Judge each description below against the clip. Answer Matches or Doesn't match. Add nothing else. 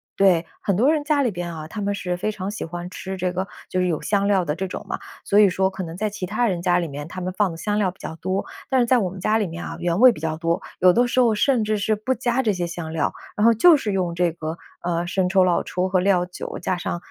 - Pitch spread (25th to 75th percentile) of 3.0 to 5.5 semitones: Matches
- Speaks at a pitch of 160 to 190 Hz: Matches